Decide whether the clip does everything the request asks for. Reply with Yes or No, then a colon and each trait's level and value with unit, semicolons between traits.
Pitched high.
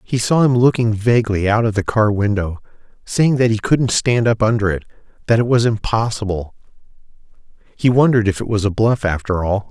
No: low, 110 Hz